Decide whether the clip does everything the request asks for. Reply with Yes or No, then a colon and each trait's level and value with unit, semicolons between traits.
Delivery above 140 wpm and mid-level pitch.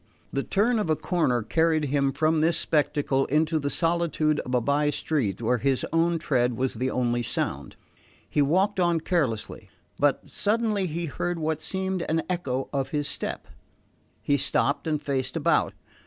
Yes: average, 170 wpm; medium, 150 Hz